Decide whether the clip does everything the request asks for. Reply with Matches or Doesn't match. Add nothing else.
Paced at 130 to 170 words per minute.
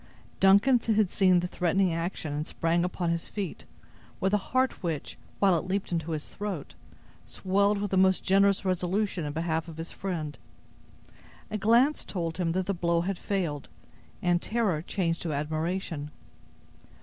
Matches